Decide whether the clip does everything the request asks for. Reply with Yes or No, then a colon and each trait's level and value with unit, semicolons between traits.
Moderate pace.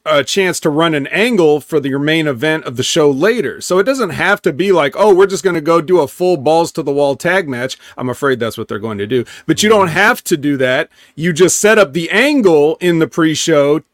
No: fast, 265 wpm